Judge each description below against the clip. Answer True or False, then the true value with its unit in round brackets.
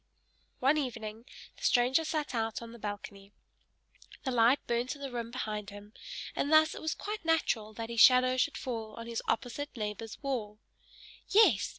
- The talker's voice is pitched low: False (235 Hz)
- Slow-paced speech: False (175 wpm)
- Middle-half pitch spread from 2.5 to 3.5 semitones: False (4.2 semitones)